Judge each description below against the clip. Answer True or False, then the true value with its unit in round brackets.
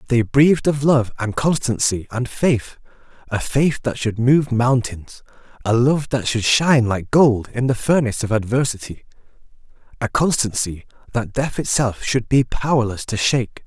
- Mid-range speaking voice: False (125 Hz)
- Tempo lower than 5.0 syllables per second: True (4.7 syllables/s)